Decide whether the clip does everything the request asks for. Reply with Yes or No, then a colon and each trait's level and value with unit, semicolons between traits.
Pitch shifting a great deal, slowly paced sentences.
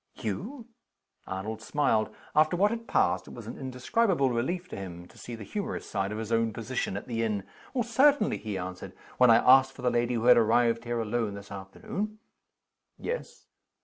No: wide, 6.1 semitones; average, 190 wpm